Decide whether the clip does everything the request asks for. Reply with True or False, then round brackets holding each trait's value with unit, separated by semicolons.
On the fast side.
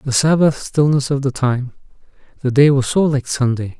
False (190 wpm)